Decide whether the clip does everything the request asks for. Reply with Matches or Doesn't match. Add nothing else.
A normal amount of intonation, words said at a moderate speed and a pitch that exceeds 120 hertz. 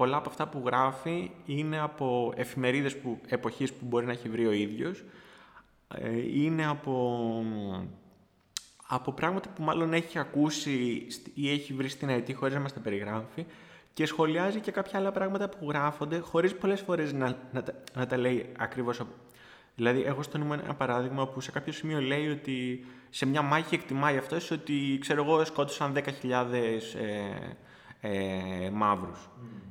Matches